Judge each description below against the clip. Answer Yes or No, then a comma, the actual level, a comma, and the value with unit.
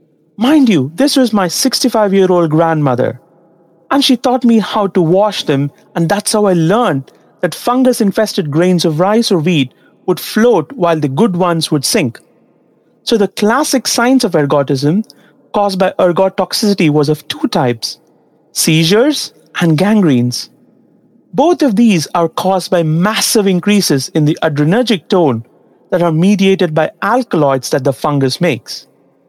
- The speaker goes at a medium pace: Yes, average, 150 wpm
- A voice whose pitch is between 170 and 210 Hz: Yes, medium, 185 Hz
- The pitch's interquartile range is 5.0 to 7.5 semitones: Yes, wide, 5.4 semitones